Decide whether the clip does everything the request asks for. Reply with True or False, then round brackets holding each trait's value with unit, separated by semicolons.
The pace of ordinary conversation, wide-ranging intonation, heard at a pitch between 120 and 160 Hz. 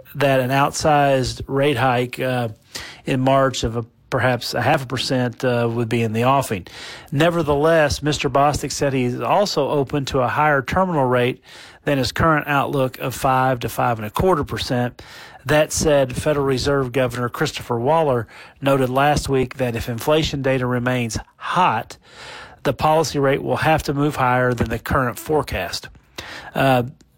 False (165 wpm; 2.9 semitones; 135 Hz)